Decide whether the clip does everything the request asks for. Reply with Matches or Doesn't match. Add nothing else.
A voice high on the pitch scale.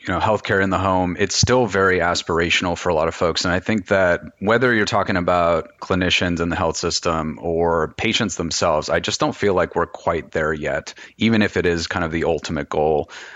Doesn't match